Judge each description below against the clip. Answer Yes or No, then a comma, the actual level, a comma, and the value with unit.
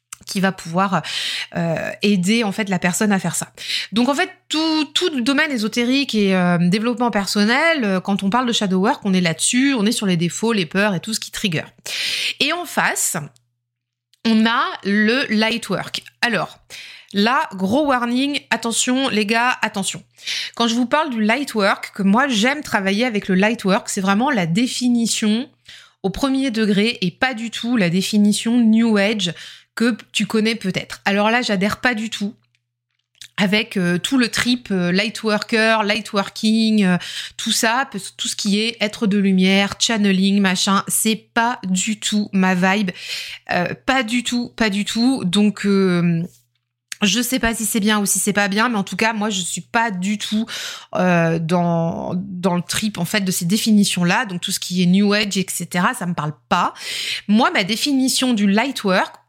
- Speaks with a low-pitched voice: No, high, 210 Hz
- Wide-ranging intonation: No, average, 3.7 semitones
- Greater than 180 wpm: Yes, average, 190 wpm